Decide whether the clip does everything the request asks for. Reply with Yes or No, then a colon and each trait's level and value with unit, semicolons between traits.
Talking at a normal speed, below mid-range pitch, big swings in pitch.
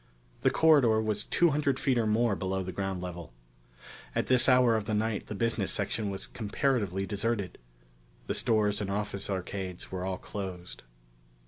No: average, 165 wpm; low, 105 Hz; average, 3.4 semitones